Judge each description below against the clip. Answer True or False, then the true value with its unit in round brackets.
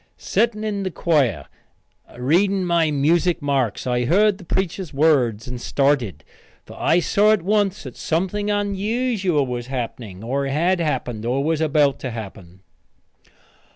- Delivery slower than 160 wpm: True (145 wpm)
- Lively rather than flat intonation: True (7.3 semitones)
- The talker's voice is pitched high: False (155 Hz)